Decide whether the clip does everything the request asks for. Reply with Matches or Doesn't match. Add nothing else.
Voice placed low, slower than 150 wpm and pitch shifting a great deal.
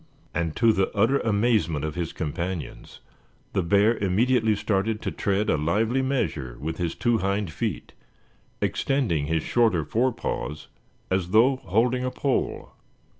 Matches